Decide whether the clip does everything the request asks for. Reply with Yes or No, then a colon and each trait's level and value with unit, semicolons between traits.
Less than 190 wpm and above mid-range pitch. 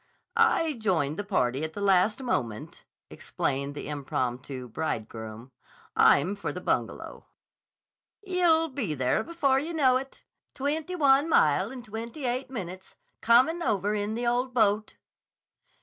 Yes: slow, 135 wpm; high, 215 Hz